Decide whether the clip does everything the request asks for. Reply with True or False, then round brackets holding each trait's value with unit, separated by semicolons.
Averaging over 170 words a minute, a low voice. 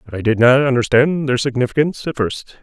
True (205 wpm; 130 Hz)